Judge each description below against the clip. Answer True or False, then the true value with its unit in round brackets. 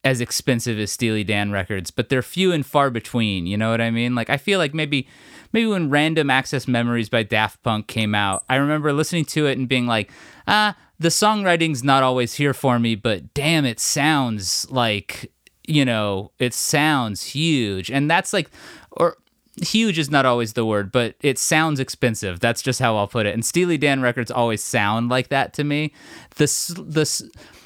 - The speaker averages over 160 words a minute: True (195 wpm)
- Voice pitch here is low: True (130 Hz)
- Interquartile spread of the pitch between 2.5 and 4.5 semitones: False (5.1 semitones)